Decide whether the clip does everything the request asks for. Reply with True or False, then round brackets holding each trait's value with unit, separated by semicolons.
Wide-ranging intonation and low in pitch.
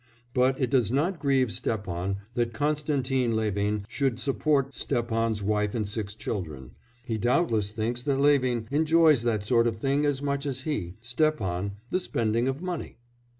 False (4.6 semitones; 120 Hz)